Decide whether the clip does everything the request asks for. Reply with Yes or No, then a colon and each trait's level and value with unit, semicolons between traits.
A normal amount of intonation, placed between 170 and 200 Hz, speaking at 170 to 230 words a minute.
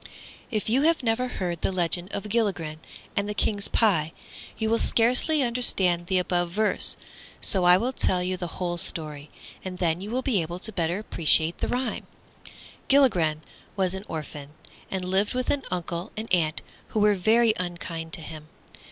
Yes: average, 4.4 semitones; medium, 185 Hz; average, 180 wpm